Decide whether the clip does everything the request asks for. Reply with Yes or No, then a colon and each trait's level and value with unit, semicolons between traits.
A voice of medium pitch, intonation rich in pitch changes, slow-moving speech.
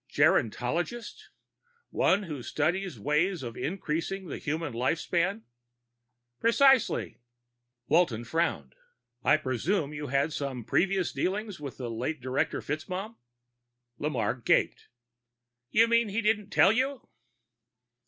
Yes: medium, 165 Hz; wide, 6.1 semitones; slow, 115 wpm